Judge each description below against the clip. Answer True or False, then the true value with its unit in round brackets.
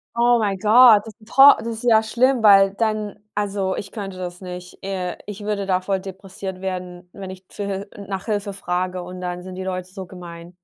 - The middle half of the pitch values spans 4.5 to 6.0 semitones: False (2.4 semitones)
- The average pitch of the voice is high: True (195 Hz)